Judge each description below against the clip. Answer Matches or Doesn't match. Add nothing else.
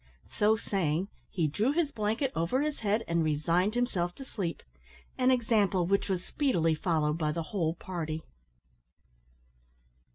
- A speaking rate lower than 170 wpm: Matches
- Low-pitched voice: Doesn't match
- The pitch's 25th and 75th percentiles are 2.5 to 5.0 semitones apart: Doesn't match